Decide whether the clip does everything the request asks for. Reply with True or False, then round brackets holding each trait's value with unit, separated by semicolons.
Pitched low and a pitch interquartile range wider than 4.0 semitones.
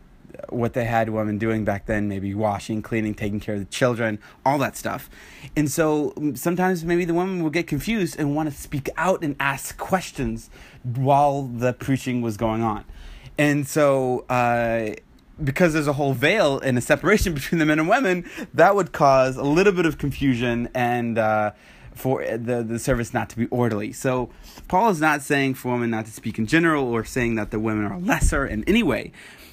True (130 Hz; 4.9 semitones)